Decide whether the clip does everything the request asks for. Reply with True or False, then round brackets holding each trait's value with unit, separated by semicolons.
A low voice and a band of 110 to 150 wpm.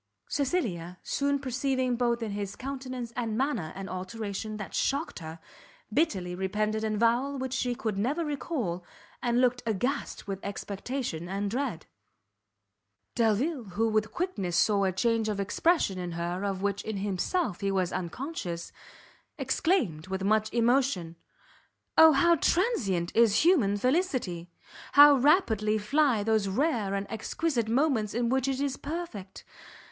False (225 Hz; 140 wpm)